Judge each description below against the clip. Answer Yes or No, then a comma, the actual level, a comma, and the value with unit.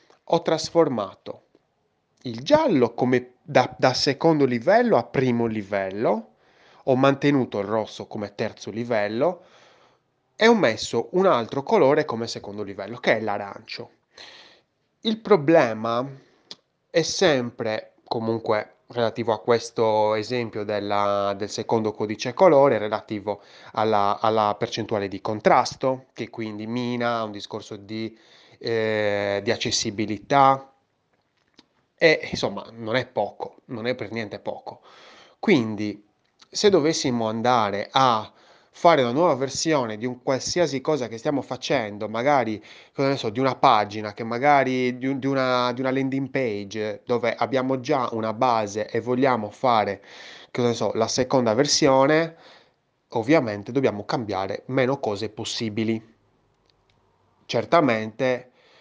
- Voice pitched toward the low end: Yes, low, 120 Hz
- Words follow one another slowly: No, average, 125 wpm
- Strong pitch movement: No, average, 3.6 semitones